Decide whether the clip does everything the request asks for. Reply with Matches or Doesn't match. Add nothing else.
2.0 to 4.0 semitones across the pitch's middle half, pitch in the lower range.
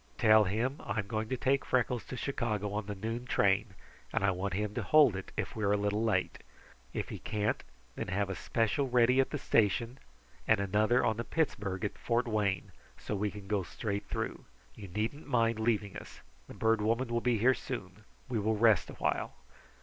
Matches